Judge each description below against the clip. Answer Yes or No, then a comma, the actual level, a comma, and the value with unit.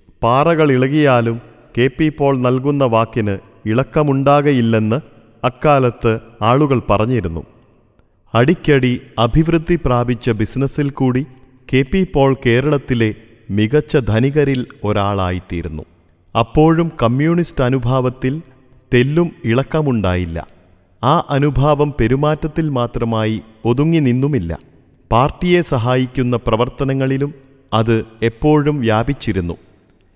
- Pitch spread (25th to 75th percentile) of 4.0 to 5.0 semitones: Yes, average, 4.3 semitones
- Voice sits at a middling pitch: No, low, 125 Hz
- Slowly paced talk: No, average, 80 wpm